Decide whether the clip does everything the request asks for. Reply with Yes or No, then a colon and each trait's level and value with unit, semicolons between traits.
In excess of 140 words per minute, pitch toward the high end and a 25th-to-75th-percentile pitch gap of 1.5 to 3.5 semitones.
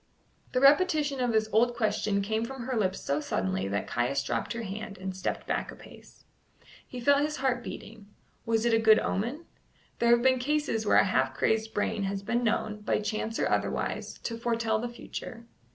Yes: average, 200 wpm; high, 225 Hz; average, 3.2 semitones